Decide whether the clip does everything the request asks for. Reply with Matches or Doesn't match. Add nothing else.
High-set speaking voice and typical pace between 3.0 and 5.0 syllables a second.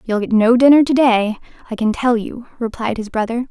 Doesn't match